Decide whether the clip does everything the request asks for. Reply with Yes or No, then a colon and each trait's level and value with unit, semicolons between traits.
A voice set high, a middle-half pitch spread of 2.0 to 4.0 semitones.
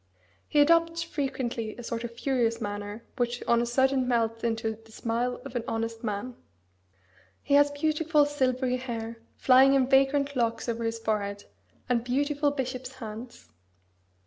Yes: high, 245 Hz; average, 3.1 semitones